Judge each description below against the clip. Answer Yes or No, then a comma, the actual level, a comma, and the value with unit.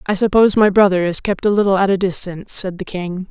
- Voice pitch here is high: Yes, high, 195 Hz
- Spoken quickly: Yes, fast, 255 wpm